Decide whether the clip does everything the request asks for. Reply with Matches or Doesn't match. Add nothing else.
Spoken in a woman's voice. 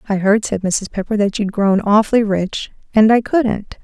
Matches